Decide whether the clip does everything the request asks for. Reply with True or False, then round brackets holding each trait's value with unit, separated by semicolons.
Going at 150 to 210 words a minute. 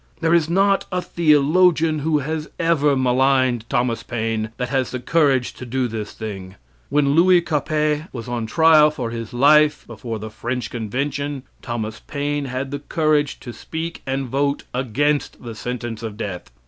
True (165 wpm)